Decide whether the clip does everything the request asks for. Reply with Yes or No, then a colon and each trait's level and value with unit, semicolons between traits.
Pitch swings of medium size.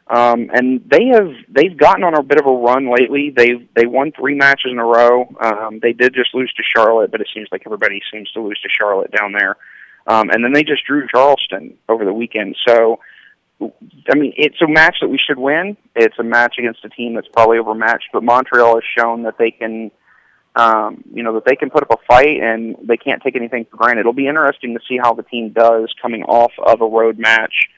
No: narrow, 2.2 semitones